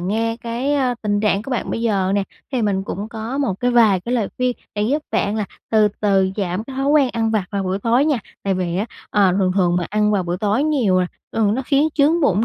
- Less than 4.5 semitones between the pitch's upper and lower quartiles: Yes, average, 4.1 semitones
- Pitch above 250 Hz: No, high, 215 Hz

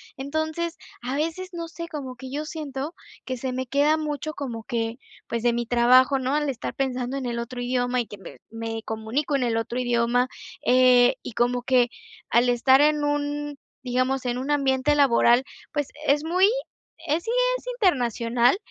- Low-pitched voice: No, very high, 260 Hz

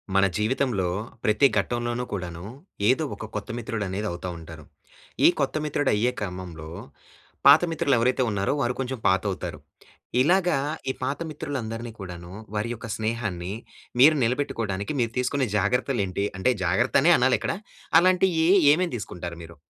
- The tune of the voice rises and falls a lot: Yes, wide, 5.7 semitones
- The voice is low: Yes, low, 115 Hz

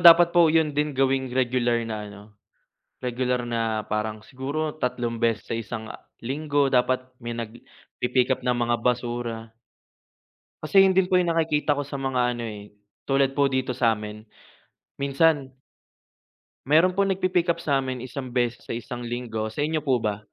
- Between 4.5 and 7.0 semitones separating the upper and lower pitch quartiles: No, average, 3.8 semitones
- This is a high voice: No, low, 130 Hz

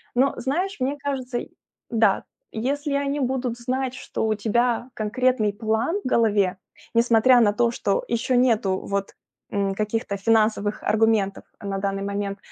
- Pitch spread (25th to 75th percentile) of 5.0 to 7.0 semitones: No, average, 3.8 semitones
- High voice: Yes, high, 225 Hz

